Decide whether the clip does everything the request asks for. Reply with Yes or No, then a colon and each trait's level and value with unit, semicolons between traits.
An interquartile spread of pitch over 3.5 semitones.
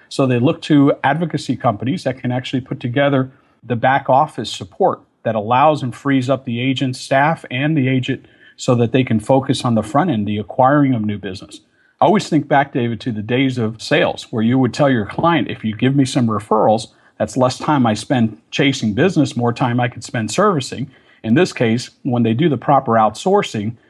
No: average, 3.1 semitones